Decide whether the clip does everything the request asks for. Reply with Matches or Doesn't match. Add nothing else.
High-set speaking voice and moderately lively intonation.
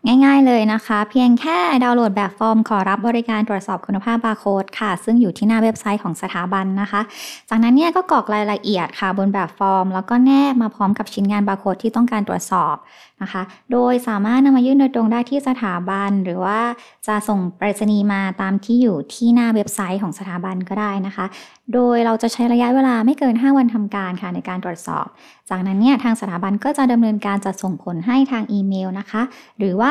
Matches